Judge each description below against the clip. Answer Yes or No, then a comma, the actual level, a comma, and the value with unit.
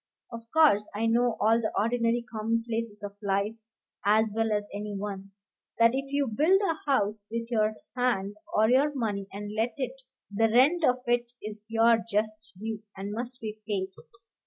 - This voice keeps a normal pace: Yes, average, 175 wpm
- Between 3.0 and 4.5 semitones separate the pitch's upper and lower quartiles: No, narrow, 2.5 semitones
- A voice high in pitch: Yes, high, 225 Hz